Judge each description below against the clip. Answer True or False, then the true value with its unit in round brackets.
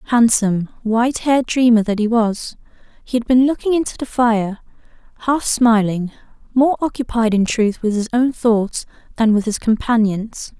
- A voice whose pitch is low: False (230 Hz)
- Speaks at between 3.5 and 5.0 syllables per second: True (4.8 syllables/s)